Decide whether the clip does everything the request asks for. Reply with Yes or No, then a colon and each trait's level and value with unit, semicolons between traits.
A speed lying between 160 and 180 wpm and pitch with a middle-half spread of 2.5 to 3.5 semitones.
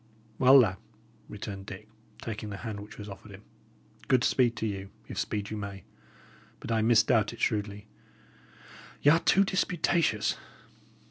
No: average, 150 wpm; average, 2.9 semitones